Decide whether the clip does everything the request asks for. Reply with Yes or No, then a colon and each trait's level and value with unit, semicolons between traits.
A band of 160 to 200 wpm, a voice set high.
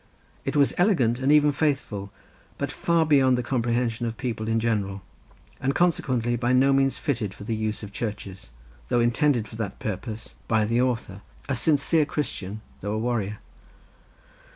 No: average, 165 wpm; low, 120 Hz